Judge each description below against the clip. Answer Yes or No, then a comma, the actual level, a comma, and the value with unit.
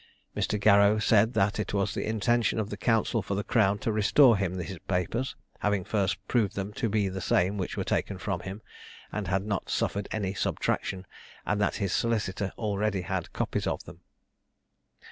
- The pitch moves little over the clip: Yes, narrow, 1.9 semitones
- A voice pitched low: Yes, low, 100 Hz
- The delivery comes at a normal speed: Yes, average, 185 wpm